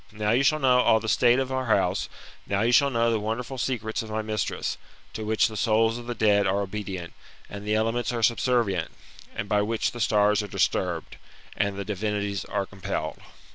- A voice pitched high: No, low, 110 Hz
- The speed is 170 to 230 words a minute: Yes, fast, 205 wpm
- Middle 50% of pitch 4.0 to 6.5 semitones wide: No, narrow, 2.5 semitones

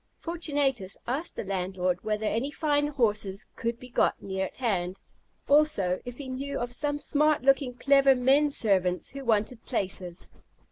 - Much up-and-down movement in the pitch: Yes, wide, 6.2 semitones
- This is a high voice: Yes, high, 245 Hz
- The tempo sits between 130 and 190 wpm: Yes, average, 155 wpm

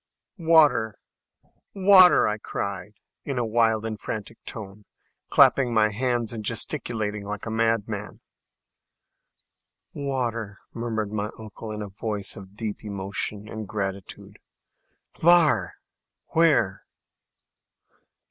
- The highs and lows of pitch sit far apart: No, narrow, 2.4 semitones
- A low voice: Yes, low, 110 Hz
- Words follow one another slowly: Yes, slow, 105 wpm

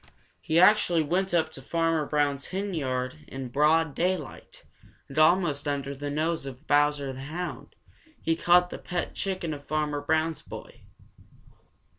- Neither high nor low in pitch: Yes, medium, 155 Hz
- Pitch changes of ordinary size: Yes, average, 3.0 semitones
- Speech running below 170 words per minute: Yes, average, 145 wpm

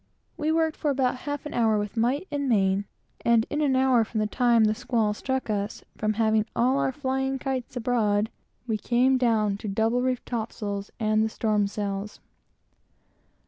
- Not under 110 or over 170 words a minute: No, average, 185 wpm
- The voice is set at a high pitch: Yes, high, 230 Hz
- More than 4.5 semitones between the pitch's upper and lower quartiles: No, average, 3.6 semitones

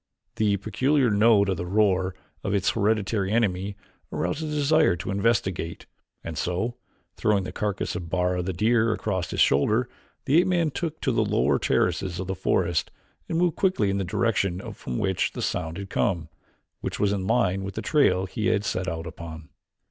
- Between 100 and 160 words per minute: No, average, 185 wpm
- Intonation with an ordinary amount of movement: Yes, average, 4.1 semitones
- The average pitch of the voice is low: Yes, low, 100 Hz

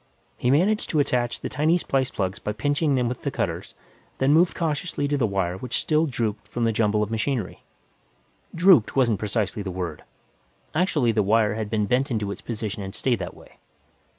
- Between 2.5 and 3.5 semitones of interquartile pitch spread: No, average, 5.3 semitones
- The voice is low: Yes, low, 120 Hz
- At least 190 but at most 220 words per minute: Yes, average, 195 wpm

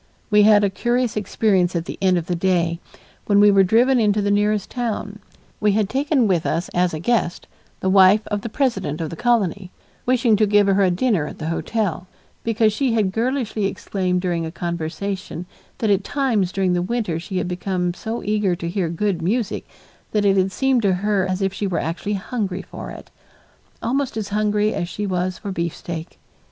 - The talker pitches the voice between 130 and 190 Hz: No, high, 200 Hz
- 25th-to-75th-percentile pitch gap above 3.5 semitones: No, average, 3.2 semitones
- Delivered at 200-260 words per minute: Yes, fast, 205 wpm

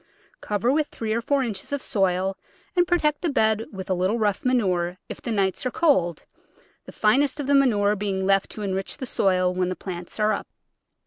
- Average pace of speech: No, fast, 210 wpm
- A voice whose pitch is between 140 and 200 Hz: No, high, 210 Hz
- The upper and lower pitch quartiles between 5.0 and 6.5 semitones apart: Yes, average, 5.3 semitones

